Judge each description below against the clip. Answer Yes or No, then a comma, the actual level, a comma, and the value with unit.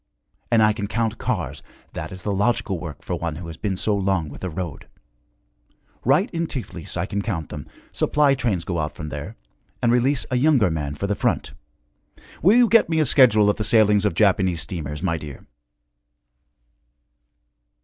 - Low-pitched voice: Yes, low, 100 Hz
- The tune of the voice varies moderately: No, wide, 6.1 semitones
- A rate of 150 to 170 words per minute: No, average, 185 wpm